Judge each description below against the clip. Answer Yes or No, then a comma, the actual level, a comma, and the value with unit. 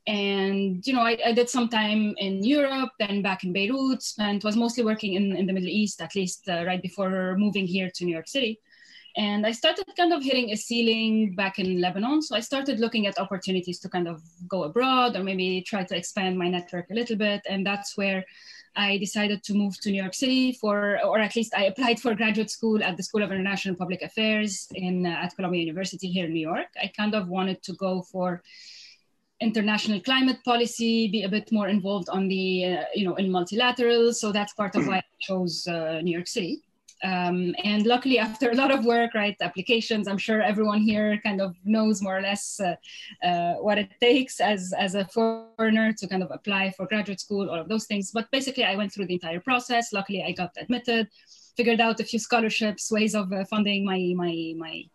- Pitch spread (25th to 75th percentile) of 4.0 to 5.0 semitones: No, average, 3.3 semitones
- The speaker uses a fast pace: Yes, fast, 215 wpm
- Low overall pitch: No, high, 205 Hz